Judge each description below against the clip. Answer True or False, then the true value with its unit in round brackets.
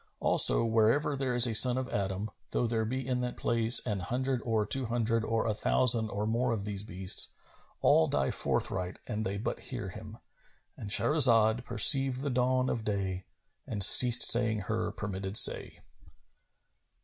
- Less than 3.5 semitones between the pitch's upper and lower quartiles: True (3.0 semitones)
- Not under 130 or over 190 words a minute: True (165 wpm)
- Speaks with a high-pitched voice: False (115 Hz)